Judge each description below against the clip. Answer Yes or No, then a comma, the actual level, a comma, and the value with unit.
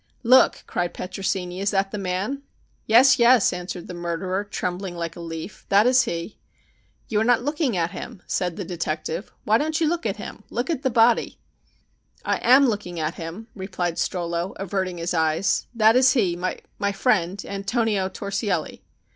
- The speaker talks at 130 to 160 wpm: No, average, 170 wpm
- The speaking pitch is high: Yes, high, 195 Hz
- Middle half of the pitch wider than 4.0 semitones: Yes, average, 4.6 semitones